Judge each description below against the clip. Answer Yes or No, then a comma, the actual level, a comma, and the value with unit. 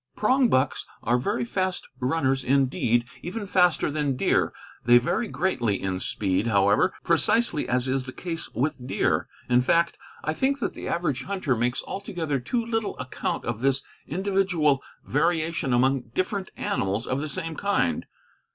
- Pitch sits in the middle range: Yes, medium, 145 Hz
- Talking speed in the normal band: Yes, average, 150 wpm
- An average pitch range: No, wide, 6.8 semitones